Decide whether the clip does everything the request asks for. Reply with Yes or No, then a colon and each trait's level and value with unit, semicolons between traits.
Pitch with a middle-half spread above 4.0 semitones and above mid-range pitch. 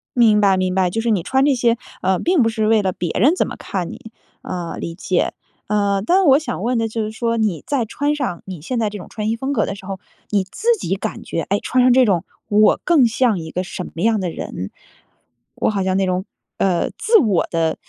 Yes: average, 4.4 semitones; high, 210 Hz